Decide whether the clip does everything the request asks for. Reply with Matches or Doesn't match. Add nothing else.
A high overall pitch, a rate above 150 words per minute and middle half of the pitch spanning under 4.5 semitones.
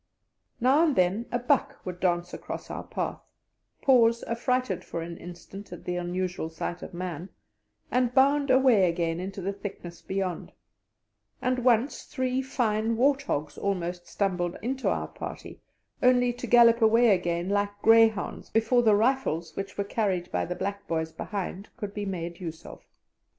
Doesn't match